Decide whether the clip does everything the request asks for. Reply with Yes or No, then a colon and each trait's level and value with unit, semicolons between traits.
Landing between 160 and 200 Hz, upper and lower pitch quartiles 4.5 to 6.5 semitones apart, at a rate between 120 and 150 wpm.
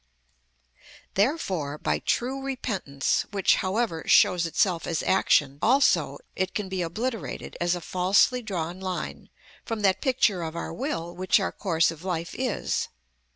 Yes: medium, 185 Hz; average, 5.0 semitones; average, 145 wpm